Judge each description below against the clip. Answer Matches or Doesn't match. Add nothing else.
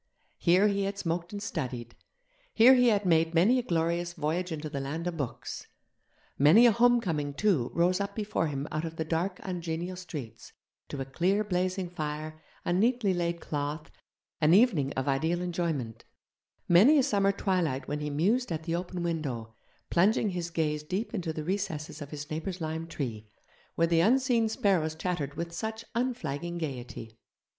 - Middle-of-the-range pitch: Matches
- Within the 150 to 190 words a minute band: Matches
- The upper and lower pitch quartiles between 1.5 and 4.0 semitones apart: Doesn't match